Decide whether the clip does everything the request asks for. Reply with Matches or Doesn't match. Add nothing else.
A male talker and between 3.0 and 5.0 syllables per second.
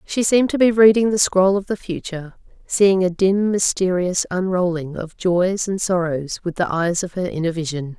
Doesn't match